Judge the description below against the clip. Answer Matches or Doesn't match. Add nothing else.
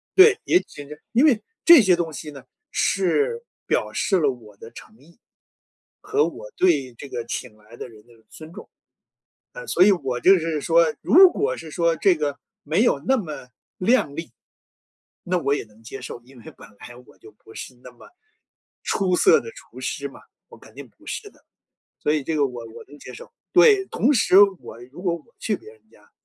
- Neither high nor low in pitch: Matches